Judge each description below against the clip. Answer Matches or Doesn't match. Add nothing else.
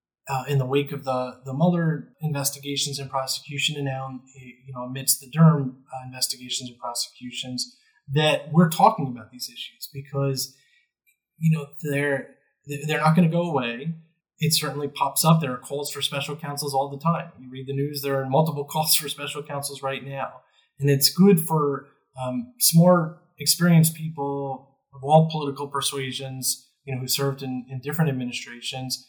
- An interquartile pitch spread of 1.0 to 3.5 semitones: Matches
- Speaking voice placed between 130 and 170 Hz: Matches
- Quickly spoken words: Doesn't match